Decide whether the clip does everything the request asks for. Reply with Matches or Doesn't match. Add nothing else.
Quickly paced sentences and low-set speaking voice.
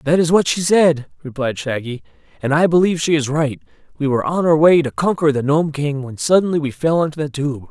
Doesn't match